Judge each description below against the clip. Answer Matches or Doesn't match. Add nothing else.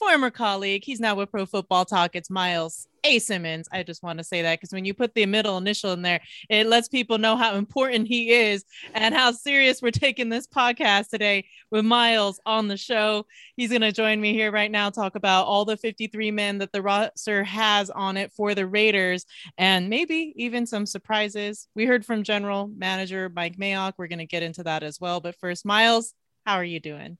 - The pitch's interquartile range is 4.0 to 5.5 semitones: Doesn't match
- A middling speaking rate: Doesn't match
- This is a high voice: Matches